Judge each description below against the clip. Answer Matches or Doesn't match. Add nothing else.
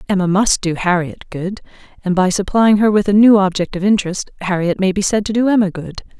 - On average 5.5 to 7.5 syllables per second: Matches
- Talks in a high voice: Matches